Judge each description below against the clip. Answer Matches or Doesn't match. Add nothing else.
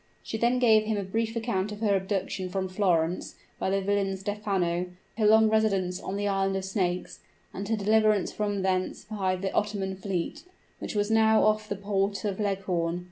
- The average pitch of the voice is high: Matches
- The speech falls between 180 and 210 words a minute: Matches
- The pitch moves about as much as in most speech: Doesn't match